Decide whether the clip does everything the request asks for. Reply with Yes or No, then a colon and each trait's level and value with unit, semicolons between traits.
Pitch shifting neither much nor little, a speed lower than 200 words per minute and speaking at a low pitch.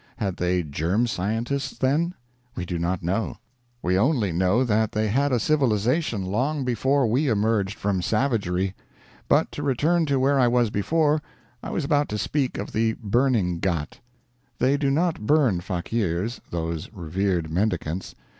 No: wide, 6.7 semitones; average, 155 wpm; low, 110 Hz